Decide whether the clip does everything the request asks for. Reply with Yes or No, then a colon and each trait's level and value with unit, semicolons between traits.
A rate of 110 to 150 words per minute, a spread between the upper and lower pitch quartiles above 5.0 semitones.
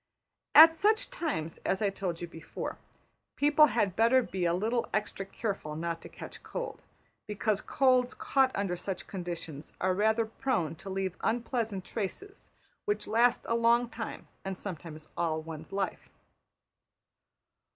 Yes: average, 145 wpm; wide, 5.6 semitones